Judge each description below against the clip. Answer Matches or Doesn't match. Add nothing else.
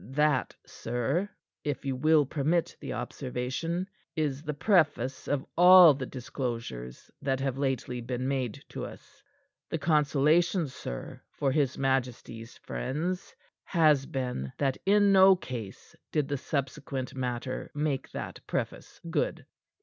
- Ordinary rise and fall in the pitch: Matches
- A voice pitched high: Doesn't match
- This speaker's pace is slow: Matches